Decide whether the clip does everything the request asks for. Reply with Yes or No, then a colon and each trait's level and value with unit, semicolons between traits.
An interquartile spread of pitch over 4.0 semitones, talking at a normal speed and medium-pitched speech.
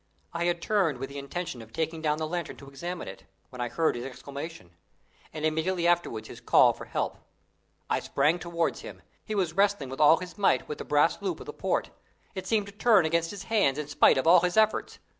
No: average, 4.4 semitones; fast, 225 wpm; medium, 165 Hz